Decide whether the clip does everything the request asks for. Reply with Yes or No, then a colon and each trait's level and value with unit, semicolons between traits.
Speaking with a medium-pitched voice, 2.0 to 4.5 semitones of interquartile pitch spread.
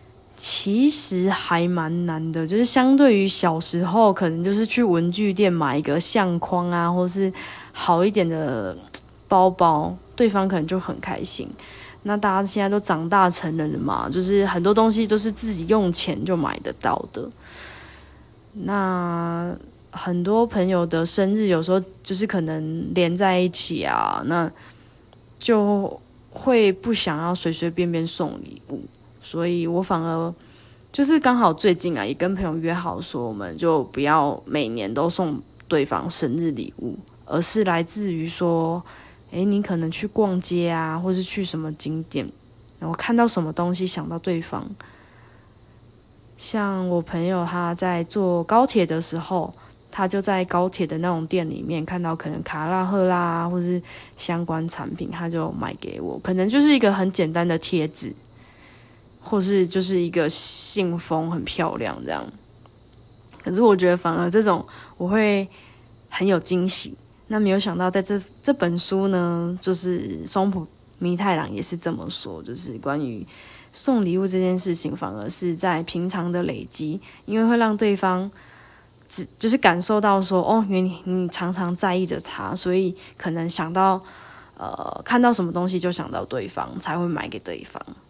Yes: medium, 180 Hz; average, 2.9 semitones